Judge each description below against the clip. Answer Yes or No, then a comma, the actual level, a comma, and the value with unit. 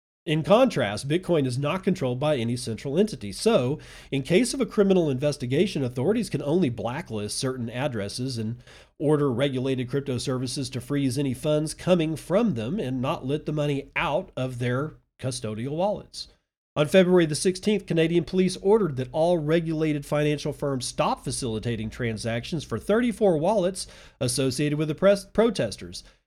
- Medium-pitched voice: Yes, medium, 145 Hz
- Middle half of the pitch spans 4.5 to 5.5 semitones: Yes, average, 5.2 semitones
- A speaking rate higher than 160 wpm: No, average, 155 wpm